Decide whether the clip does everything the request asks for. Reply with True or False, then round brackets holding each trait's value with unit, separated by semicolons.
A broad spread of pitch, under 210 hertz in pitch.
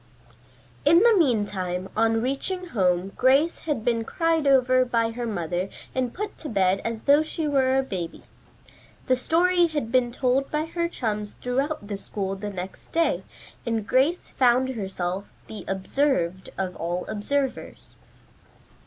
False (6.3 semitones; 245 Hz)